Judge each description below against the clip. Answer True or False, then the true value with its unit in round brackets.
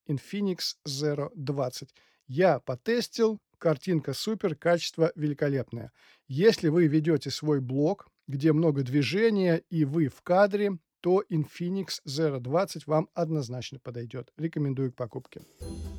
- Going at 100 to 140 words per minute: True (115 wpm)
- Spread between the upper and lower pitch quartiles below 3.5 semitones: False (4.1 semitones)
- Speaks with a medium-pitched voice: True (155 Hz)